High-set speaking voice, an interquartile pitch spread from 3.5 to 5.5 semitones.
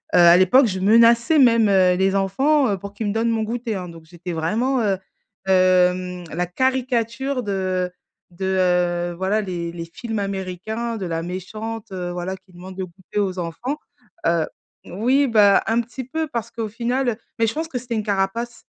Yes: high, 200 Hz; average, 4.4 semitones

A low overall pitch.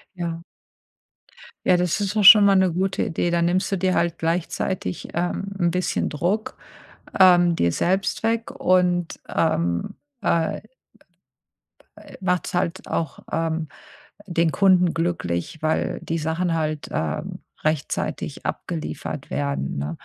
No: medium, 170 Hz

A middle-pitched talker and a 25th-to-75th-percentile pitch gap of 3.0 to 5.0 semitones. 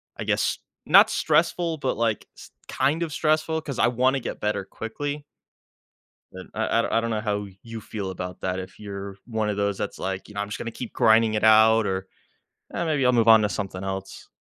No: low, 110 Hz; average, 3.7 semitones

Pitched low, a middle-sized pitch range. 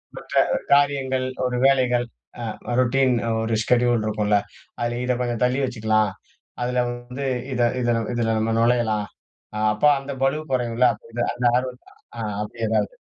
No: low, 120 Hz; narrow, 1.9 semitones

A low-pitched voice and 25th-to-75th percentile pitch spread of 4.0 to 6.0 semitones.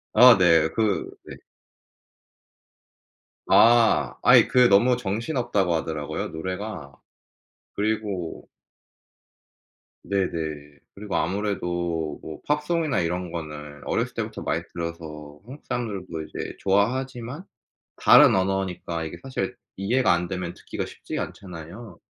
Yes: very low, 95 Hz; wide, 5.6 semitones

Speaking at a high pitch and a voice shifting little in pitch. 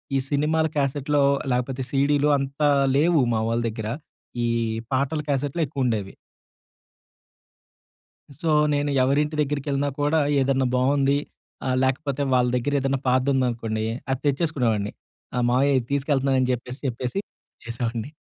No: low, 135 Hz; narrow, 2.3 semitones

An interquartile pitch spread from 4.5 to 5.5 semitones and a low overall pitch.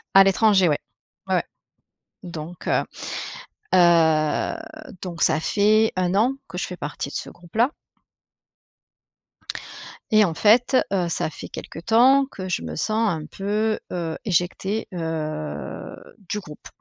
No: average, 4.9 semitones; medium, 185 Hz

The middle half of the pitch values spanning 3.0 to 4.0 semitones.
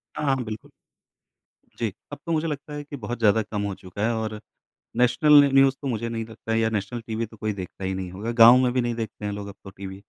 Yes: average, 3.4 semitones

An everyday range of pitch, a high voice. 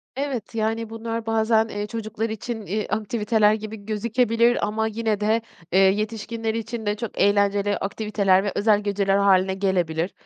No: narrow, 1.9 semitones; high, 215 Hz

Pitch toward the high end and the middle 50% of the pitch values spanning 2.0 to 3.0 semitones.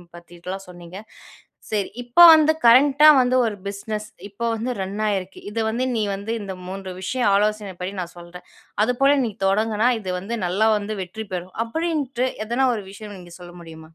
No: high, 210 Hz; average, 4.0 semitones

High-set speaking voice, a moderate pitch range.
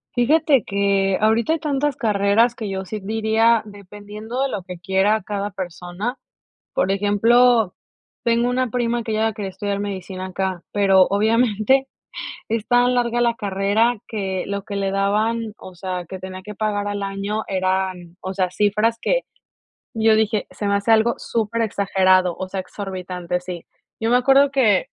Yes: high, 205 Hz; average, 3.2 semitones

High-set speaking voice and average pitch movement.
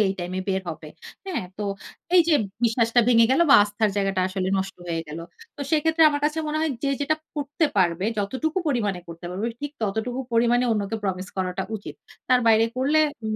No: high, 220 Hz; wide, 6.6 semitones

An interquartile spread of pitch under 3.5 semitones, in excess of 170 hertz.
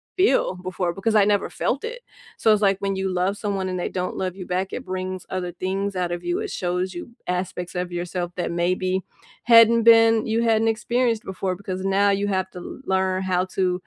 Yes: average, 2.9 semitones; high, 190 Hz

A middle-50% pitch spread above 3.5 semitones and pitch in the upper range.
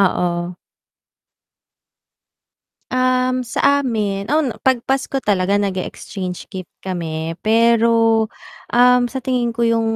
Yes: average, 4.6 semitones; high, 225 Hz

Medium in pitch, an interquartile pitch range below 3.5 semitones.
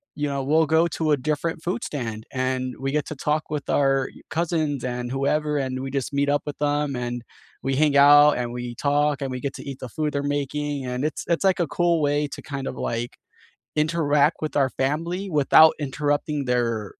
Yes: medium, 145 Hz; narrow, 2.4 semitones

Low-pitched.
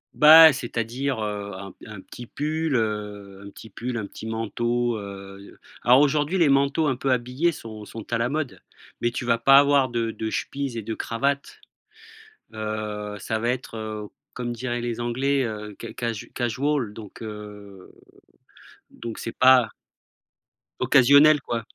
Yes: low, 120 Hz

